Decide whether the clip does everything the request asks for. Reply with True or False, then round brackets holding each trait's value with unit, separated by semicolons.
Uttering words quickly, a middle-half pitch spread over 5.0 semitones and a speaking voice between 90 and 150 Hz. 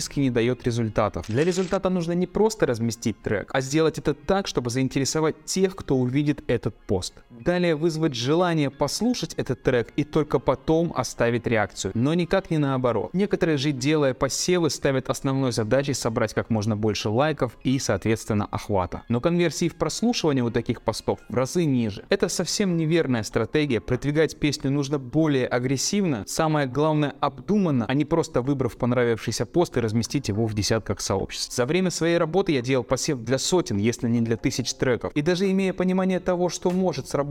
True (170 wpm; 5.6 semitones; 140 Hz)